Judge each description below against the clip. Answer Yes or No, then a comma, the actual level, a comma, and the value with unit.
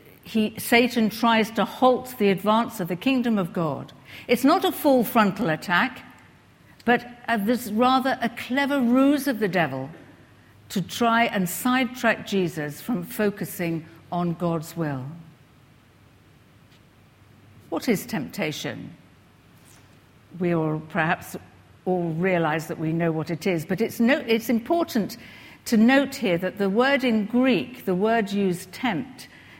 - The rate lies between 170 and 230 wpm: No, average, 140 wpm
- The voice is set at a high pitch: Yes, high, 205 Hz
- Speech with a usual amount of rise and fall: No, wide, 6.4 semitones